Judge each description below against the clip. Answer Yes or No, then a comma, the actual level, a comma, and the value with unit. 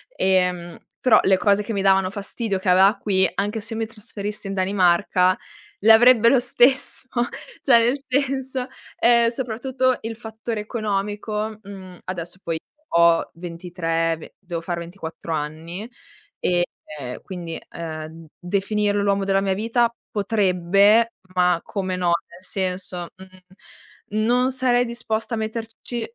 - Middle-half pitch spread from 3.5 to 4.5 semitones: Yes, average, 3.8 semitones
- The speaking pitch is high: Yes, high, 200 Hz